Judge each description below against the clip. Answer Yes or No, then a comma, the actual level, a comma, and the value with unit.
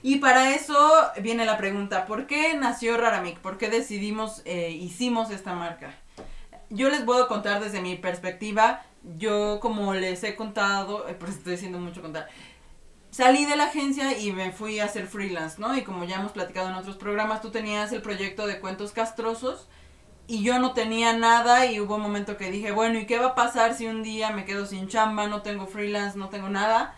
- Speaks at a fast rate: Yes, fast, 205 wpm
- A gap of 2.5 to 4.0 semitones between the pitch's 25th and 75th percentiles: Yes, average, 2.9 semitones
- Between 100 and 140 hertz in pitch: No, high, 210 Hz